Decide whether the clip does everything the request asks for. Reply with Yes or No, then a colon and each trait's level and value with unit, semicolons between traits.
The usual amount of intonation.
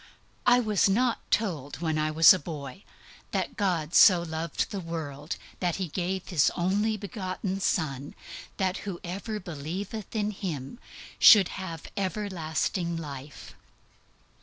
Yes: average, 4.1 semitones